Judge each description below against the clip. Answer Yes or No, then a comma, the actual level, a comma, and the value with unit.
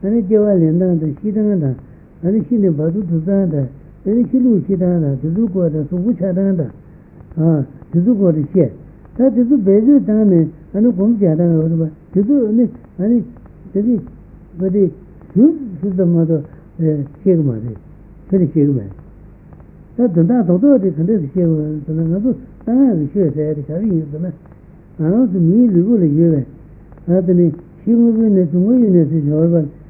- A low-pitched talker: No, medium, 180 Hz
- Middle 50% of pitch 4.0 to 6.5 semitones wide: Yes, average, 5.2 semitones